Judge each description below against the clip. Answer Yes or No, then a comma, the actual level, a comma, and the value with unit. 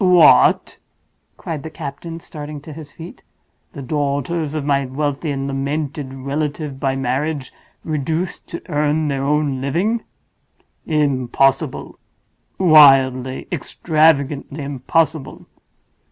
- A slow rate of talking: Yes, slow, 100 wpm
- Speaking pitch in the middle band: Yes, medium, 145 Hz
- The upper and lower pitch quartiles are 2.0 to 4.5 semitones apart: Yes, narrow, 2.4 semitones